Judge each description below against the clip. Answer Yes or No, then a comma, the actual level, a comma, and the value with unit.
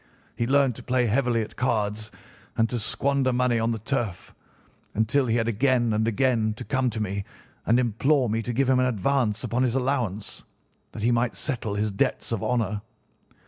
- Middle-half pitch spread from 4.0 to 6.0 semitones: No, average, 2.8 semitones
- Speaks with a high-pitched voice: No, low, 120 Hz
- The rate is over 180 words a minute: Yes, average, 190 wpm